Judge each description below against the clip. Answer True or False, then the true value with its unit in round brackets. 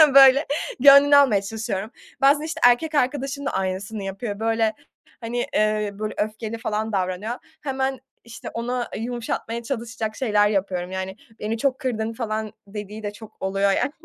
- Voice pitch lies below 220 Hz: False (225 Hz)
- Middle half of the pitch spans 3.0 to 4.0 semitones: True (3.4 semitones)